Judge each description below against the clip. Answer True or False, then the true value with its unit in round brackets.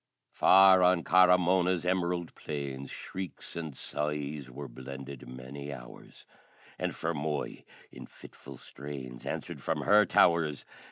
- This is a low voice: True (75 Hz)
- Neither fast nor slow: False (120 wpm)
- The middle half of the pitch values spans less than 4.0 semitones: False (4.6 semitones)